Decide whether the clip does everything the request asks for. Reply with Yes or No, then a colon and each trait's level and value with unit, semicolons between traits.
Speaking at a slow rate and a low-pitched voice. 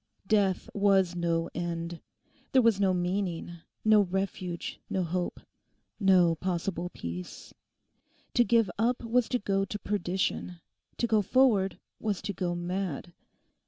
No: slow, 130 wpm; high, 190 Hz